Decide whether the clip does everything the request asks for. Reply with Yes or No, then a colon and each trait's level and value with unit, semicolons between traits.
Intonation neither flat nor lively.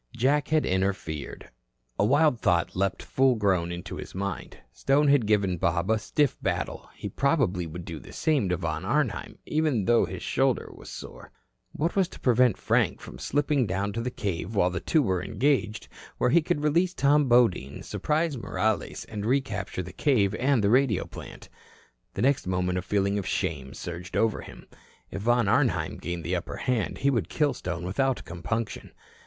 No: wide, 6.9 semitones